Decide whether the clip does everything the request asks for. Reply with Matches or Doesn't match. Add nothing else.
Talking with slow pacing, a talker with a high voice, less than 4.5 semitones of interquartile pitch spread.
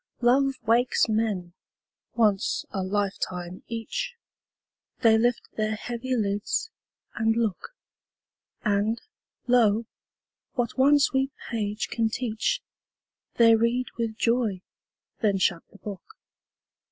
Matches